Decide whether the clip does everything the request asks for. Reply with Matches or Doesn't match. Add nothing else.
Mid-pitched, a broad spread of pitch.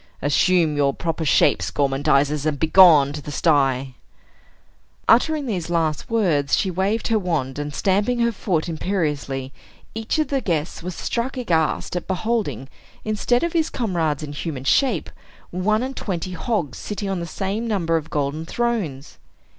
Matches